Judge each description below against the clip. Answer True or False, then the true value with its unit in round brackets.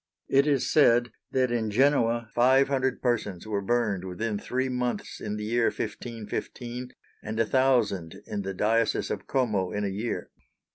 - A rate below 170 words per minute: True (160 wpm)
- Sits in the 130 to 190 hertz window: False (115 Hz)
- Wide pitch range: False (3.4 semitones)